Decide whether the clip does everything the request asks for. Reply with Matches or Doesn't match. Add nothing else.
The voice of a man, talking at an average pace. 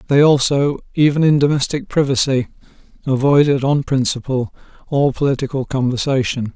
Doesn't match